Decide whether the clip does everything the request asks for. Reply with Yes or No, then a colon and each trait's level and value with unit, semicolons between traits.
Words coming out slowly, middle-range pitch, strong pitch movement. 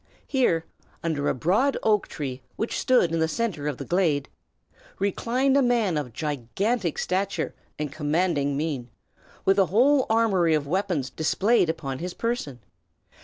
No: average, 150 wpm; medium, 175 Hz; wide, 7.0 semitones